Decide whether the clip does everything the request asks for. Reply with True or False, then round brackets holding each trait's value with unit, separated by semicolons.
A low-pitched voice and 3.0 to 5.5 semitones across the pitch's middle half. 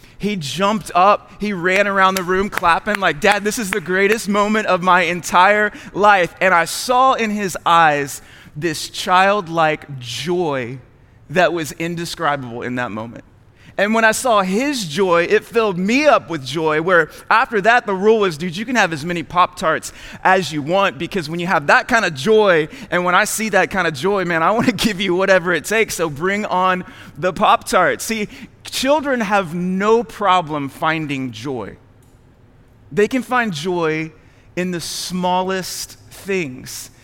False (180 Hz; 4.9 semitones)